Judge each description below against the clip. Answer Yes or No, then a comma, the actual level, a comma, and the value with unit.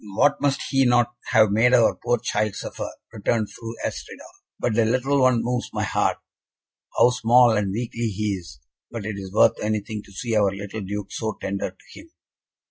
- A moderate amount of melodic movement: Yes, average, 3.0 semitones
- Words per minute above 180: Yes, average, 190 wpm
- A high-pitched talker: No, low, 110 Hz